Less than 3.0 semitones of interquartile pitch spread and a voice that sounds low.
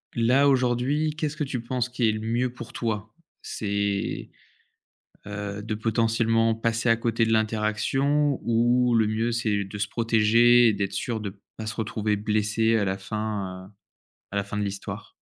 Yes: narrow, 2.4 semitones; low, 110 Hz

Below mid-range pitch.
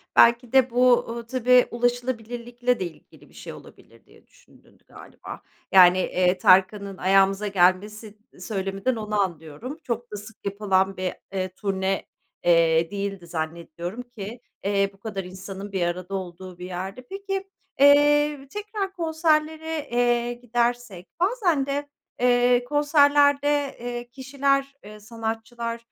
No: high, 230 Hz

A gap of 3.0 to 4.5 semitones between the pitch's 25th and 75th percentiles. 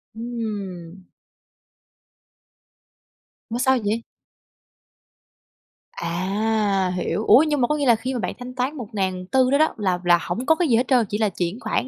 No: average, 5.1 semitones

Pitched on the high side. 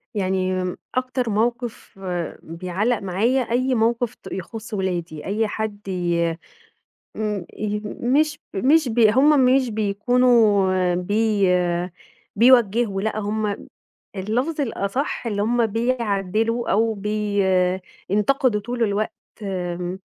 Yes: high, 215 Hz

